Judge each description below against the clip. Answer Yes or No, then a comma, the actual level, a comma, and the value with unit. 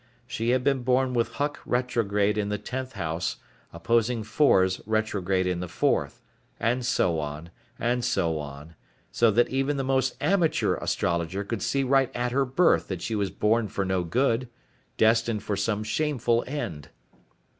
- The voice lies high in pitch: No, low, 115 Hz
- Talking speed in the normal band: Yes, average, 165 wpm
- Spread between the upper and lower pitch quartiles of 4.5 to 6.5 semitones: Yes, average, 5.1 semitones